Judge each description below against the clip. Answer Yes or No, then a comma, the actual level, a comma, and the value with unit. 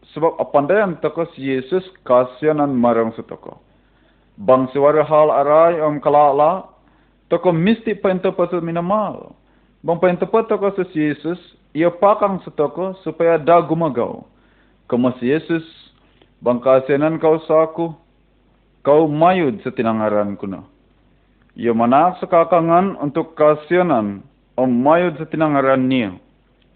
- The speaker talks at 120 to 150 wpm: Yes, average, 125 wpm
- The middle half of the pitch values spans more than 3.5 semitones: Yes, average, 4.4 semitones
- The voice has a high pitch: No, medium, 160 Hz